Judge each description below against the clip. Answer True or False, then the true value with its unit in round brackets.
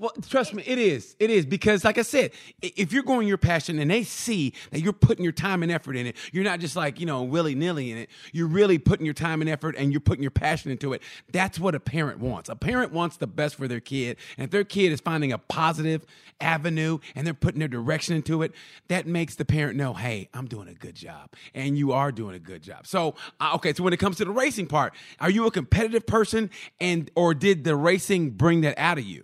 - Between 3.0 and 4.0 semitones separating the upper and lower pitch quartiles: False (5.1 semitones)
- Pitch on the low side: False (160 Hz)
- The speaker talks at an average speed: False (250 wpm)